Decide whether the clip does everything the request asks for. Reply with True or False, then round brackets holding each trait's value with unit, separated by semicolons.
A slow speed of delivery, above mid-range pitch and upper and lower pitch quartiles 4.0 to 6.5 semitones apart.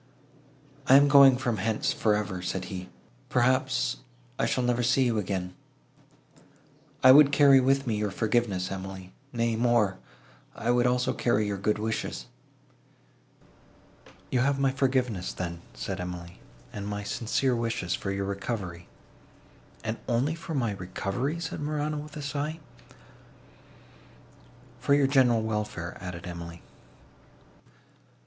False (130 wpm; 115 Hz; 5.5 semitones)